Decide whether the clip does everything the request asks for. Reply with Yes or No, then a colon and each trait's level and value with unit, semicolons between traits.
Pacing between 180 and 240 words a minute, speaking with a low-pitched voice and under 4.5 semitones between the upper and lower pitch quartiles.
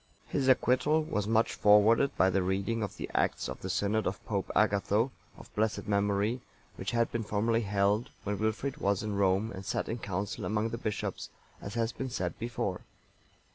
Yes: average, 190 wpm; low, 105 Hz; narrow, 2.6 semitones